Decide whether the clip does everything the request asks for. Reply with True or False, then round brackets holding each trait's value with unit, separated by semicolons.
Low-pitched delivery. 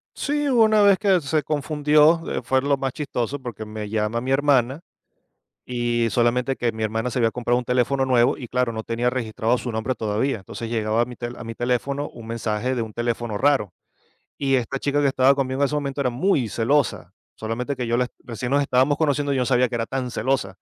True (125 Hz)